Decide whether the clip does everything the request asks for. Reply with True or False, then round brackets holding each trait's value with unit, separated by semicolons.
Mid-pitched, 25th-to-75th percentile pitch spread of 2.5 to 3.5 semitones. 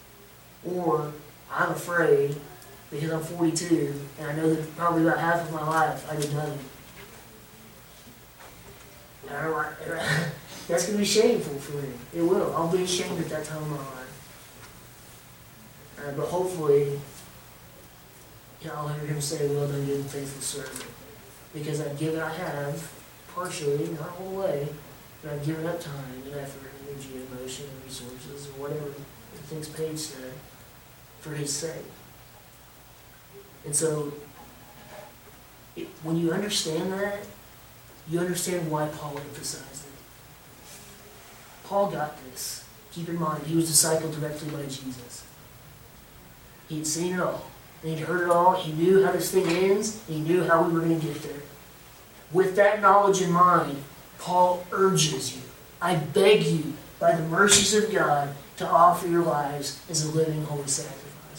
True (150 Hz; 3.1 semitones)